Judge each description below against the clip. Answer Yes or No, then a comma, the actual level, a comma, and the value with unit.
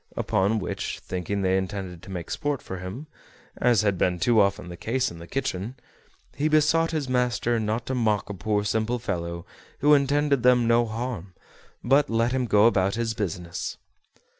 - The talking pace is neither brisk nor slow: Yes, average, 180 wpm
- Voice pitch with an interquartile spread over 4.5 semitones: Yes, average, 4.9 semitones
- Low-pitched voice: Yes, low, 110 Hz